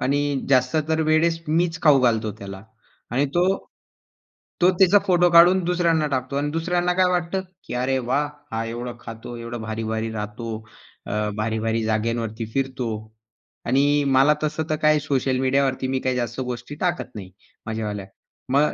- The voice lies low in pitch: Yes, low, 130 Hz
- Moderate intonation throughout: No, wide, 5.7 semitones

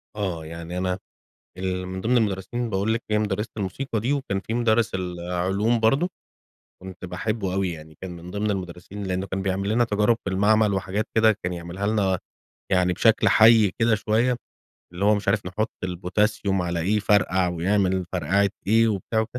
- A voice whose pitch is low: Yes, low, 100 Hz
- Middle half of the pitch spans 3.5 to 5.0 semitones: No, average, 2.9 semitones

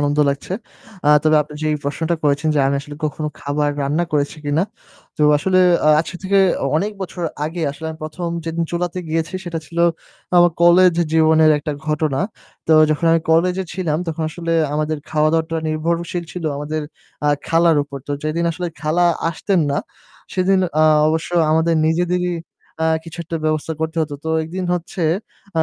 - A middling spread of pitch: No, narrow, 2.1 semitones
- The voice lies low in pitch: No, medium, 160 Hz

